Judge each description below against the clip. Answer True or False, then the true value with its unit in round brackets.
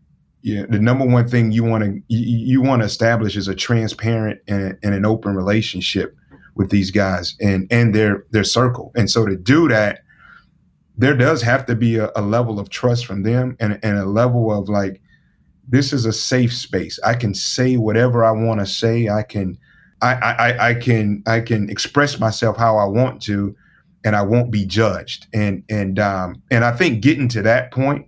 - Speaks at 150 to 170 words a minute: False (200 wpm)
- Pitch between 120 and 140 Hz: False (110 Hz)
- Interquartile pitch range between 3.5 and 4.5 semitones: False (2.8 semitones)